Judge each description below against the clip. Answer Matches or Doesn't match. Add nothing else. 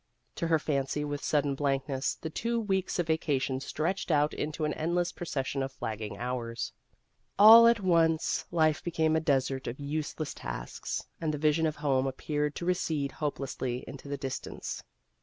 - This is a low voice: Doesn't match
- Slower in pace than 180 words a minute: Matches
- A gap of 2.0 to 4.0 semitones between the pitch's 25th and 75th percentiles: Matches